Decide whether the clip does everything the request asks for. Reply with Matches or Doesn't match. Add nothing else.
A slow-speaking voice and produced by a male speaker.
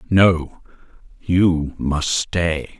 Matches